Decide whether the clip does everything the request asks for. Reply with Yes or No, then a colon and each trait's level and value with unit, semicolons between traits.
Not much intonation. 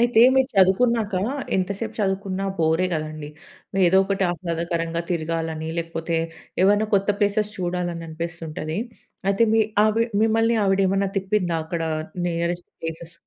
No: average, 3.4 semitones